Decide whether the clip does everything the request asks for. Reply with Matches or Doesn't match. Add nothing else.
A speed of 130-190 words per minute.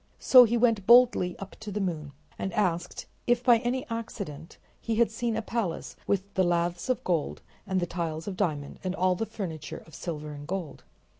Doesn't match